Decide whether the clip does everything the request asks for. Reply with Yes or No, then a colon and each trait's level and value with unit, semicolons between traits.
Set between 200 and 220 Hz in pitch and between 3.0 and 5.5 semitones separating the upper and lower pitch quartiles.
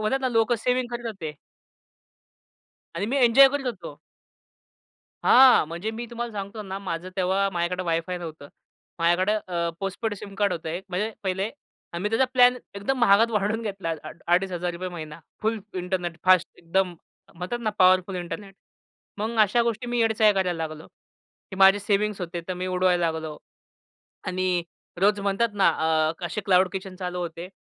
No: high, 190 Hz; average, 3.5 semitones